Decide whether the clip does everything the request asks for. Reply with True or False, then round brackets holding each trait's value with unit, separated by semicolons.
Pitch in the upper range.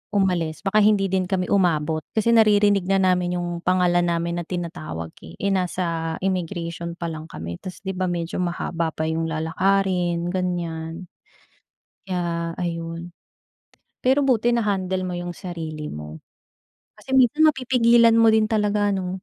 False (180 Hz)